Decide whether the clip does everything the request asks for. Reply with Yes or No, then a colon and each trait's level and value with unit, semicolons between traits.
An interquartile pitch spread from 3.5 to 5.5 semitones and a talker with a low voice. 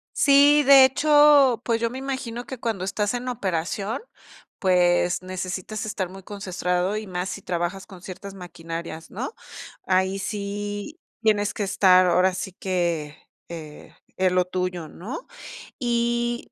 No: average, 4.6 semitones; high, 195 Hz